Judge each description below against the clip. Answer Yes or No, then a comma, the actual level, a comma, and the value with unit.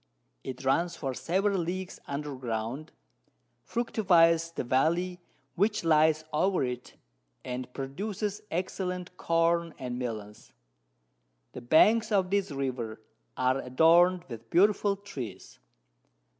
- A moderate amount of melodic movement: No, wide, 6.2 semitones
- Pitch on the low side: No, medium, 165 Hz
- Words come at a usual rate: No, slow, 110 wpm